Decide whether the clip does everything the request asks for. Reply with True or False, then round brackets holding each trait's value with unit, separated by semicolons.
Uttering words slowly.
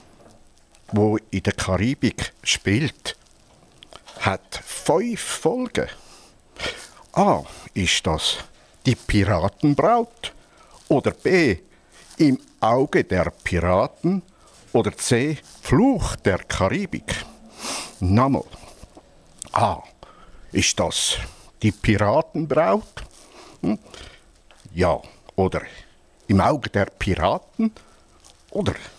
True (80 wpm)